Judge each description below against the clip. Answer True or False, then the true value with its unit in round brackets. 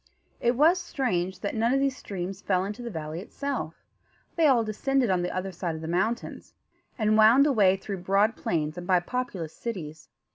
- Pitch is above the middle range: True (200 Hz)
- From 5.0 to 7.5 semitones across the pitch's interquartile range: True (5.5 semitones)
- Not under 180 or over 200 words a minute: True (190 wpm)